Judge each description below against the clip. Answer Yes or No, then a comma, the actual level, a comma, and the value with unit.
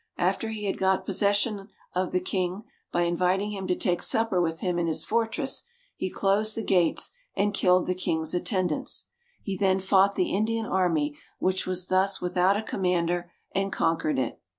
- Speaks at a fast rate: No, average, 175 wpm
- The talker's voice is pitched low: No, medium, 185 Hz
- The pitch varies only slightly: Yes, narrow, 2.1 semitones